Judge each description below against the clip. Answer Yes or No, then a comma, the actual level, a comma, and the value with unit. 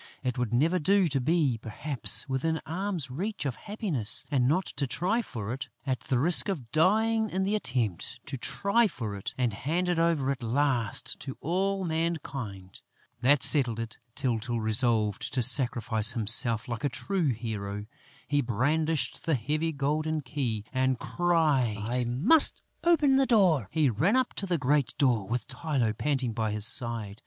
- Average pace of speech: Yes, average, 170 wpm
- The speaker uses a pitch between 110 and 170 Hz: Yes, low, 135 Hz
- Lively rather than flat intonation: Yes, wide, 6.1 semitones